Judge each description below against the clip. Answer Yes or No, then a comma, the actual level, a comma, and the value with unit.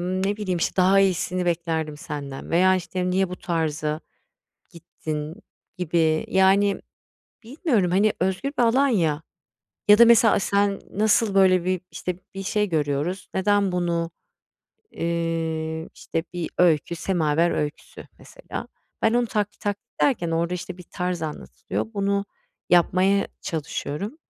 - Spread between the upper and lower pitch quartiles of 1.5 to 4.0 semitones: Yes, average, 3.3 semitones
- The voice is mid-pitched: Yes, medium, 180 Hz